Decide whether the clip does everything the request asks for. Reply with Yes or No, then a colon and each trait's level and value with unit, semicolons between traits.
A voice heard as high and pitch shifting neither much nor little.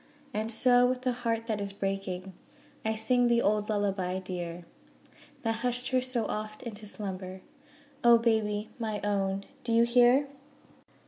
Yes: high, 220 Hz; average, 3.3 semitones